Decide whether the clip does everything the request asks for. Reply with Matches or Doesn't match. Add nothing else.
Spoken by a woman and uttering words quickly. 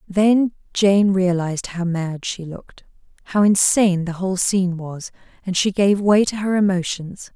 Doesn't match